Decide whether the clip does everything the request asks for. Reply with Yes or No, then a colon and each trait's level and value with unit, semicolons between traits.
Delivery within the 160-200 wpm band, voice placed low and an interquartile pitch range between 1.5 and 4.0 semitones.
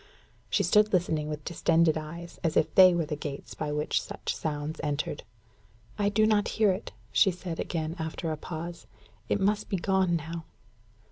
No: average, 180 wpm; medium, 170 Hz; average, 3.5 semitones